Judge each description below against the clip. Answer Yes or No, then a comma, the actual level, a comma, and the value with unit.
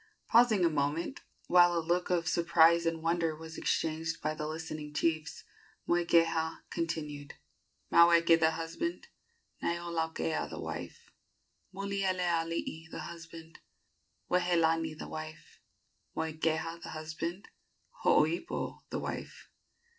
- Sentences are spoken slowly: Yes, slow, 110 wpm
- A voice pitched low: No, medium, 165 Hz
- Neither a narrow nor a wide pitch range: No, narrow, 1.3 semitones